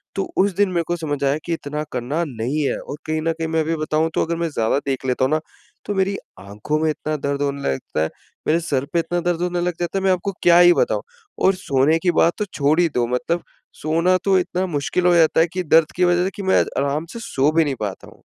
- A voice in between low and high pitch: Yes, medium, 160 Hz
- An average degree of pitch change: Yes, average, 3.7 semitones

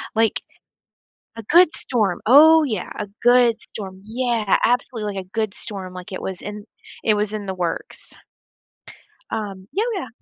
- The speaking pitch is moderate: No, high, 215 Hz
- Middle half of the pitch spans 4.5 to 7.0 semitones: No, average, 4.1 semitones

